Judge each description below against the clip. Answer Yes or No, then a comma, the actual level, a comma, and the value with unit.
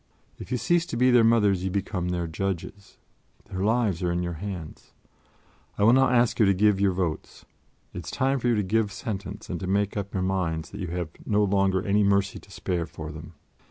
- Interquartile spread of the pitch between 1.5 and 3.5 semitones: Yes, average, 3.0 semitones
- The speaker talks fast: Yes, fast, 225 wpm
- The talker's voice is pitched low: Yes, low, 100 Hz